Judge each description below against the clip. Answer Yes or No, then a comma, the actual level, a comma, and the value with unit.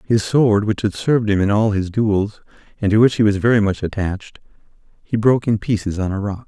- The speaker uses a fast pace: Yes, fast, 230 wpm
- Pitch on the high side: No, low, 105 Hz